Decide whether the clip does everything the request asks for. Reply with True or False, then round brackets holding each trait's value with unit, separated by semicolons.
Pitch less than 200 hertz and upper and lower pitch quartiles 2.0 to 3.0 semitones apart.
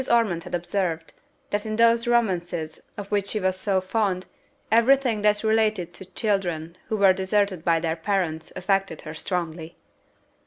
False (190 Hz; 3.8 semitones)